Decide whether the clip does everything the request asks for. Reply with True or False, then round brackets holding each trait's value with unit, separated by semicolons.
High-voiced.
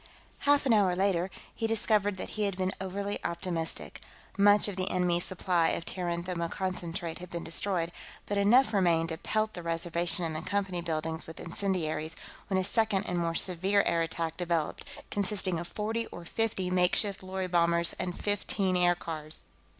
False (180 Hz)